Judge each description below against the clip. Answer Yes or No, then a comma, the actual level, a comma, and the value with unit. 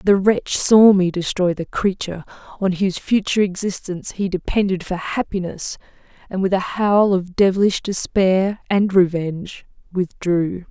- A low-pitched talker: No, high, 190 Hz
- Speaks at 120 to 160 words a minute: Yes, average, 140 wpm